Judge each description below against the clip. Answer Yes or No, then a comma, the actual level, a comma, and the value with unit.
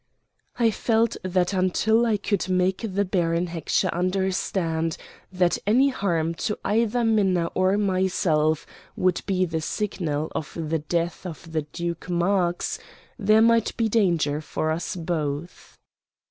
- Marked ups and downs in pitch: No, average, 3.5 semitones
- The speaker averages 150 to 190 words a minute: No, slow, 135 wpm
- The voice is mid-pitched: Yes, medium, 180 Hz